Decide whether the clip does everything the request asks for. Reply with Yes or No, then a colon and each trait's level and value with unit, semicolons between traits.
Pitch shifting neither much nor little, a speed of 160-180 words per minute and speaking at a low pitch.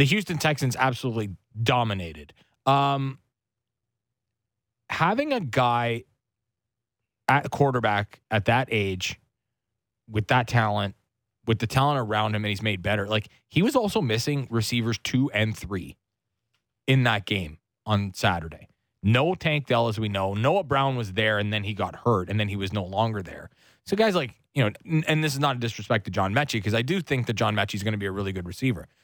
No: average, 4.1 semitones; average, 190 wpm; low, 115 Hz